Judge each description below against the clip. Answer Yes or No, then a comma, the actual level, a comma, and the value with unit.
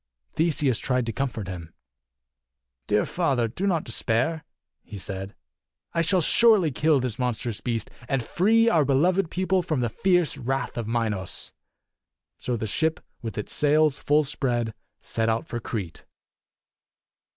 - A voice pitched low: Yes, low, 130 Hz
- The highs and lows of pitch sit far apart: Yes, wide, 6.1 semitones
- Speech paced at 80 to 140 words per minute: No, average, 150 wpm